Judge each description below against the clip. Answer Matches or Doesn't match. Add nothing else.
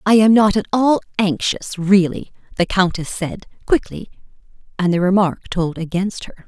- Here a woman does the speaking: Matches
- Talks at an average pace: Matches